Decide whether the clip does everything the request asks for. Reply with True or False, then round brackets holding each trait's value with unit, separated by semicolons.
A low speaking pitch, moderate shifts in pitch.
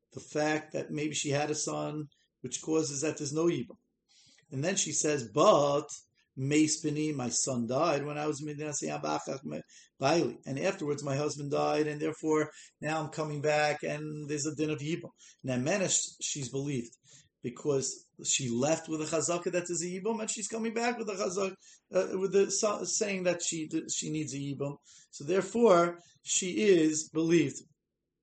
False (155 Hz; 3.0 semitones)